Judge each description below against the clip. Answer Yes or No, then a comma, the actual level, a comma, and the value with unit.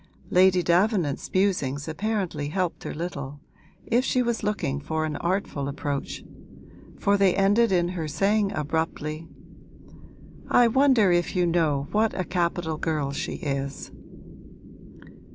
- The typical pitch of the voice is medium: Yes, medium, 175 Hz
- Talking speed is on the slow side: Yes, slow, 130 wpm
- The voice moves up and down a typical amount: Yes, average, 4.8 semitones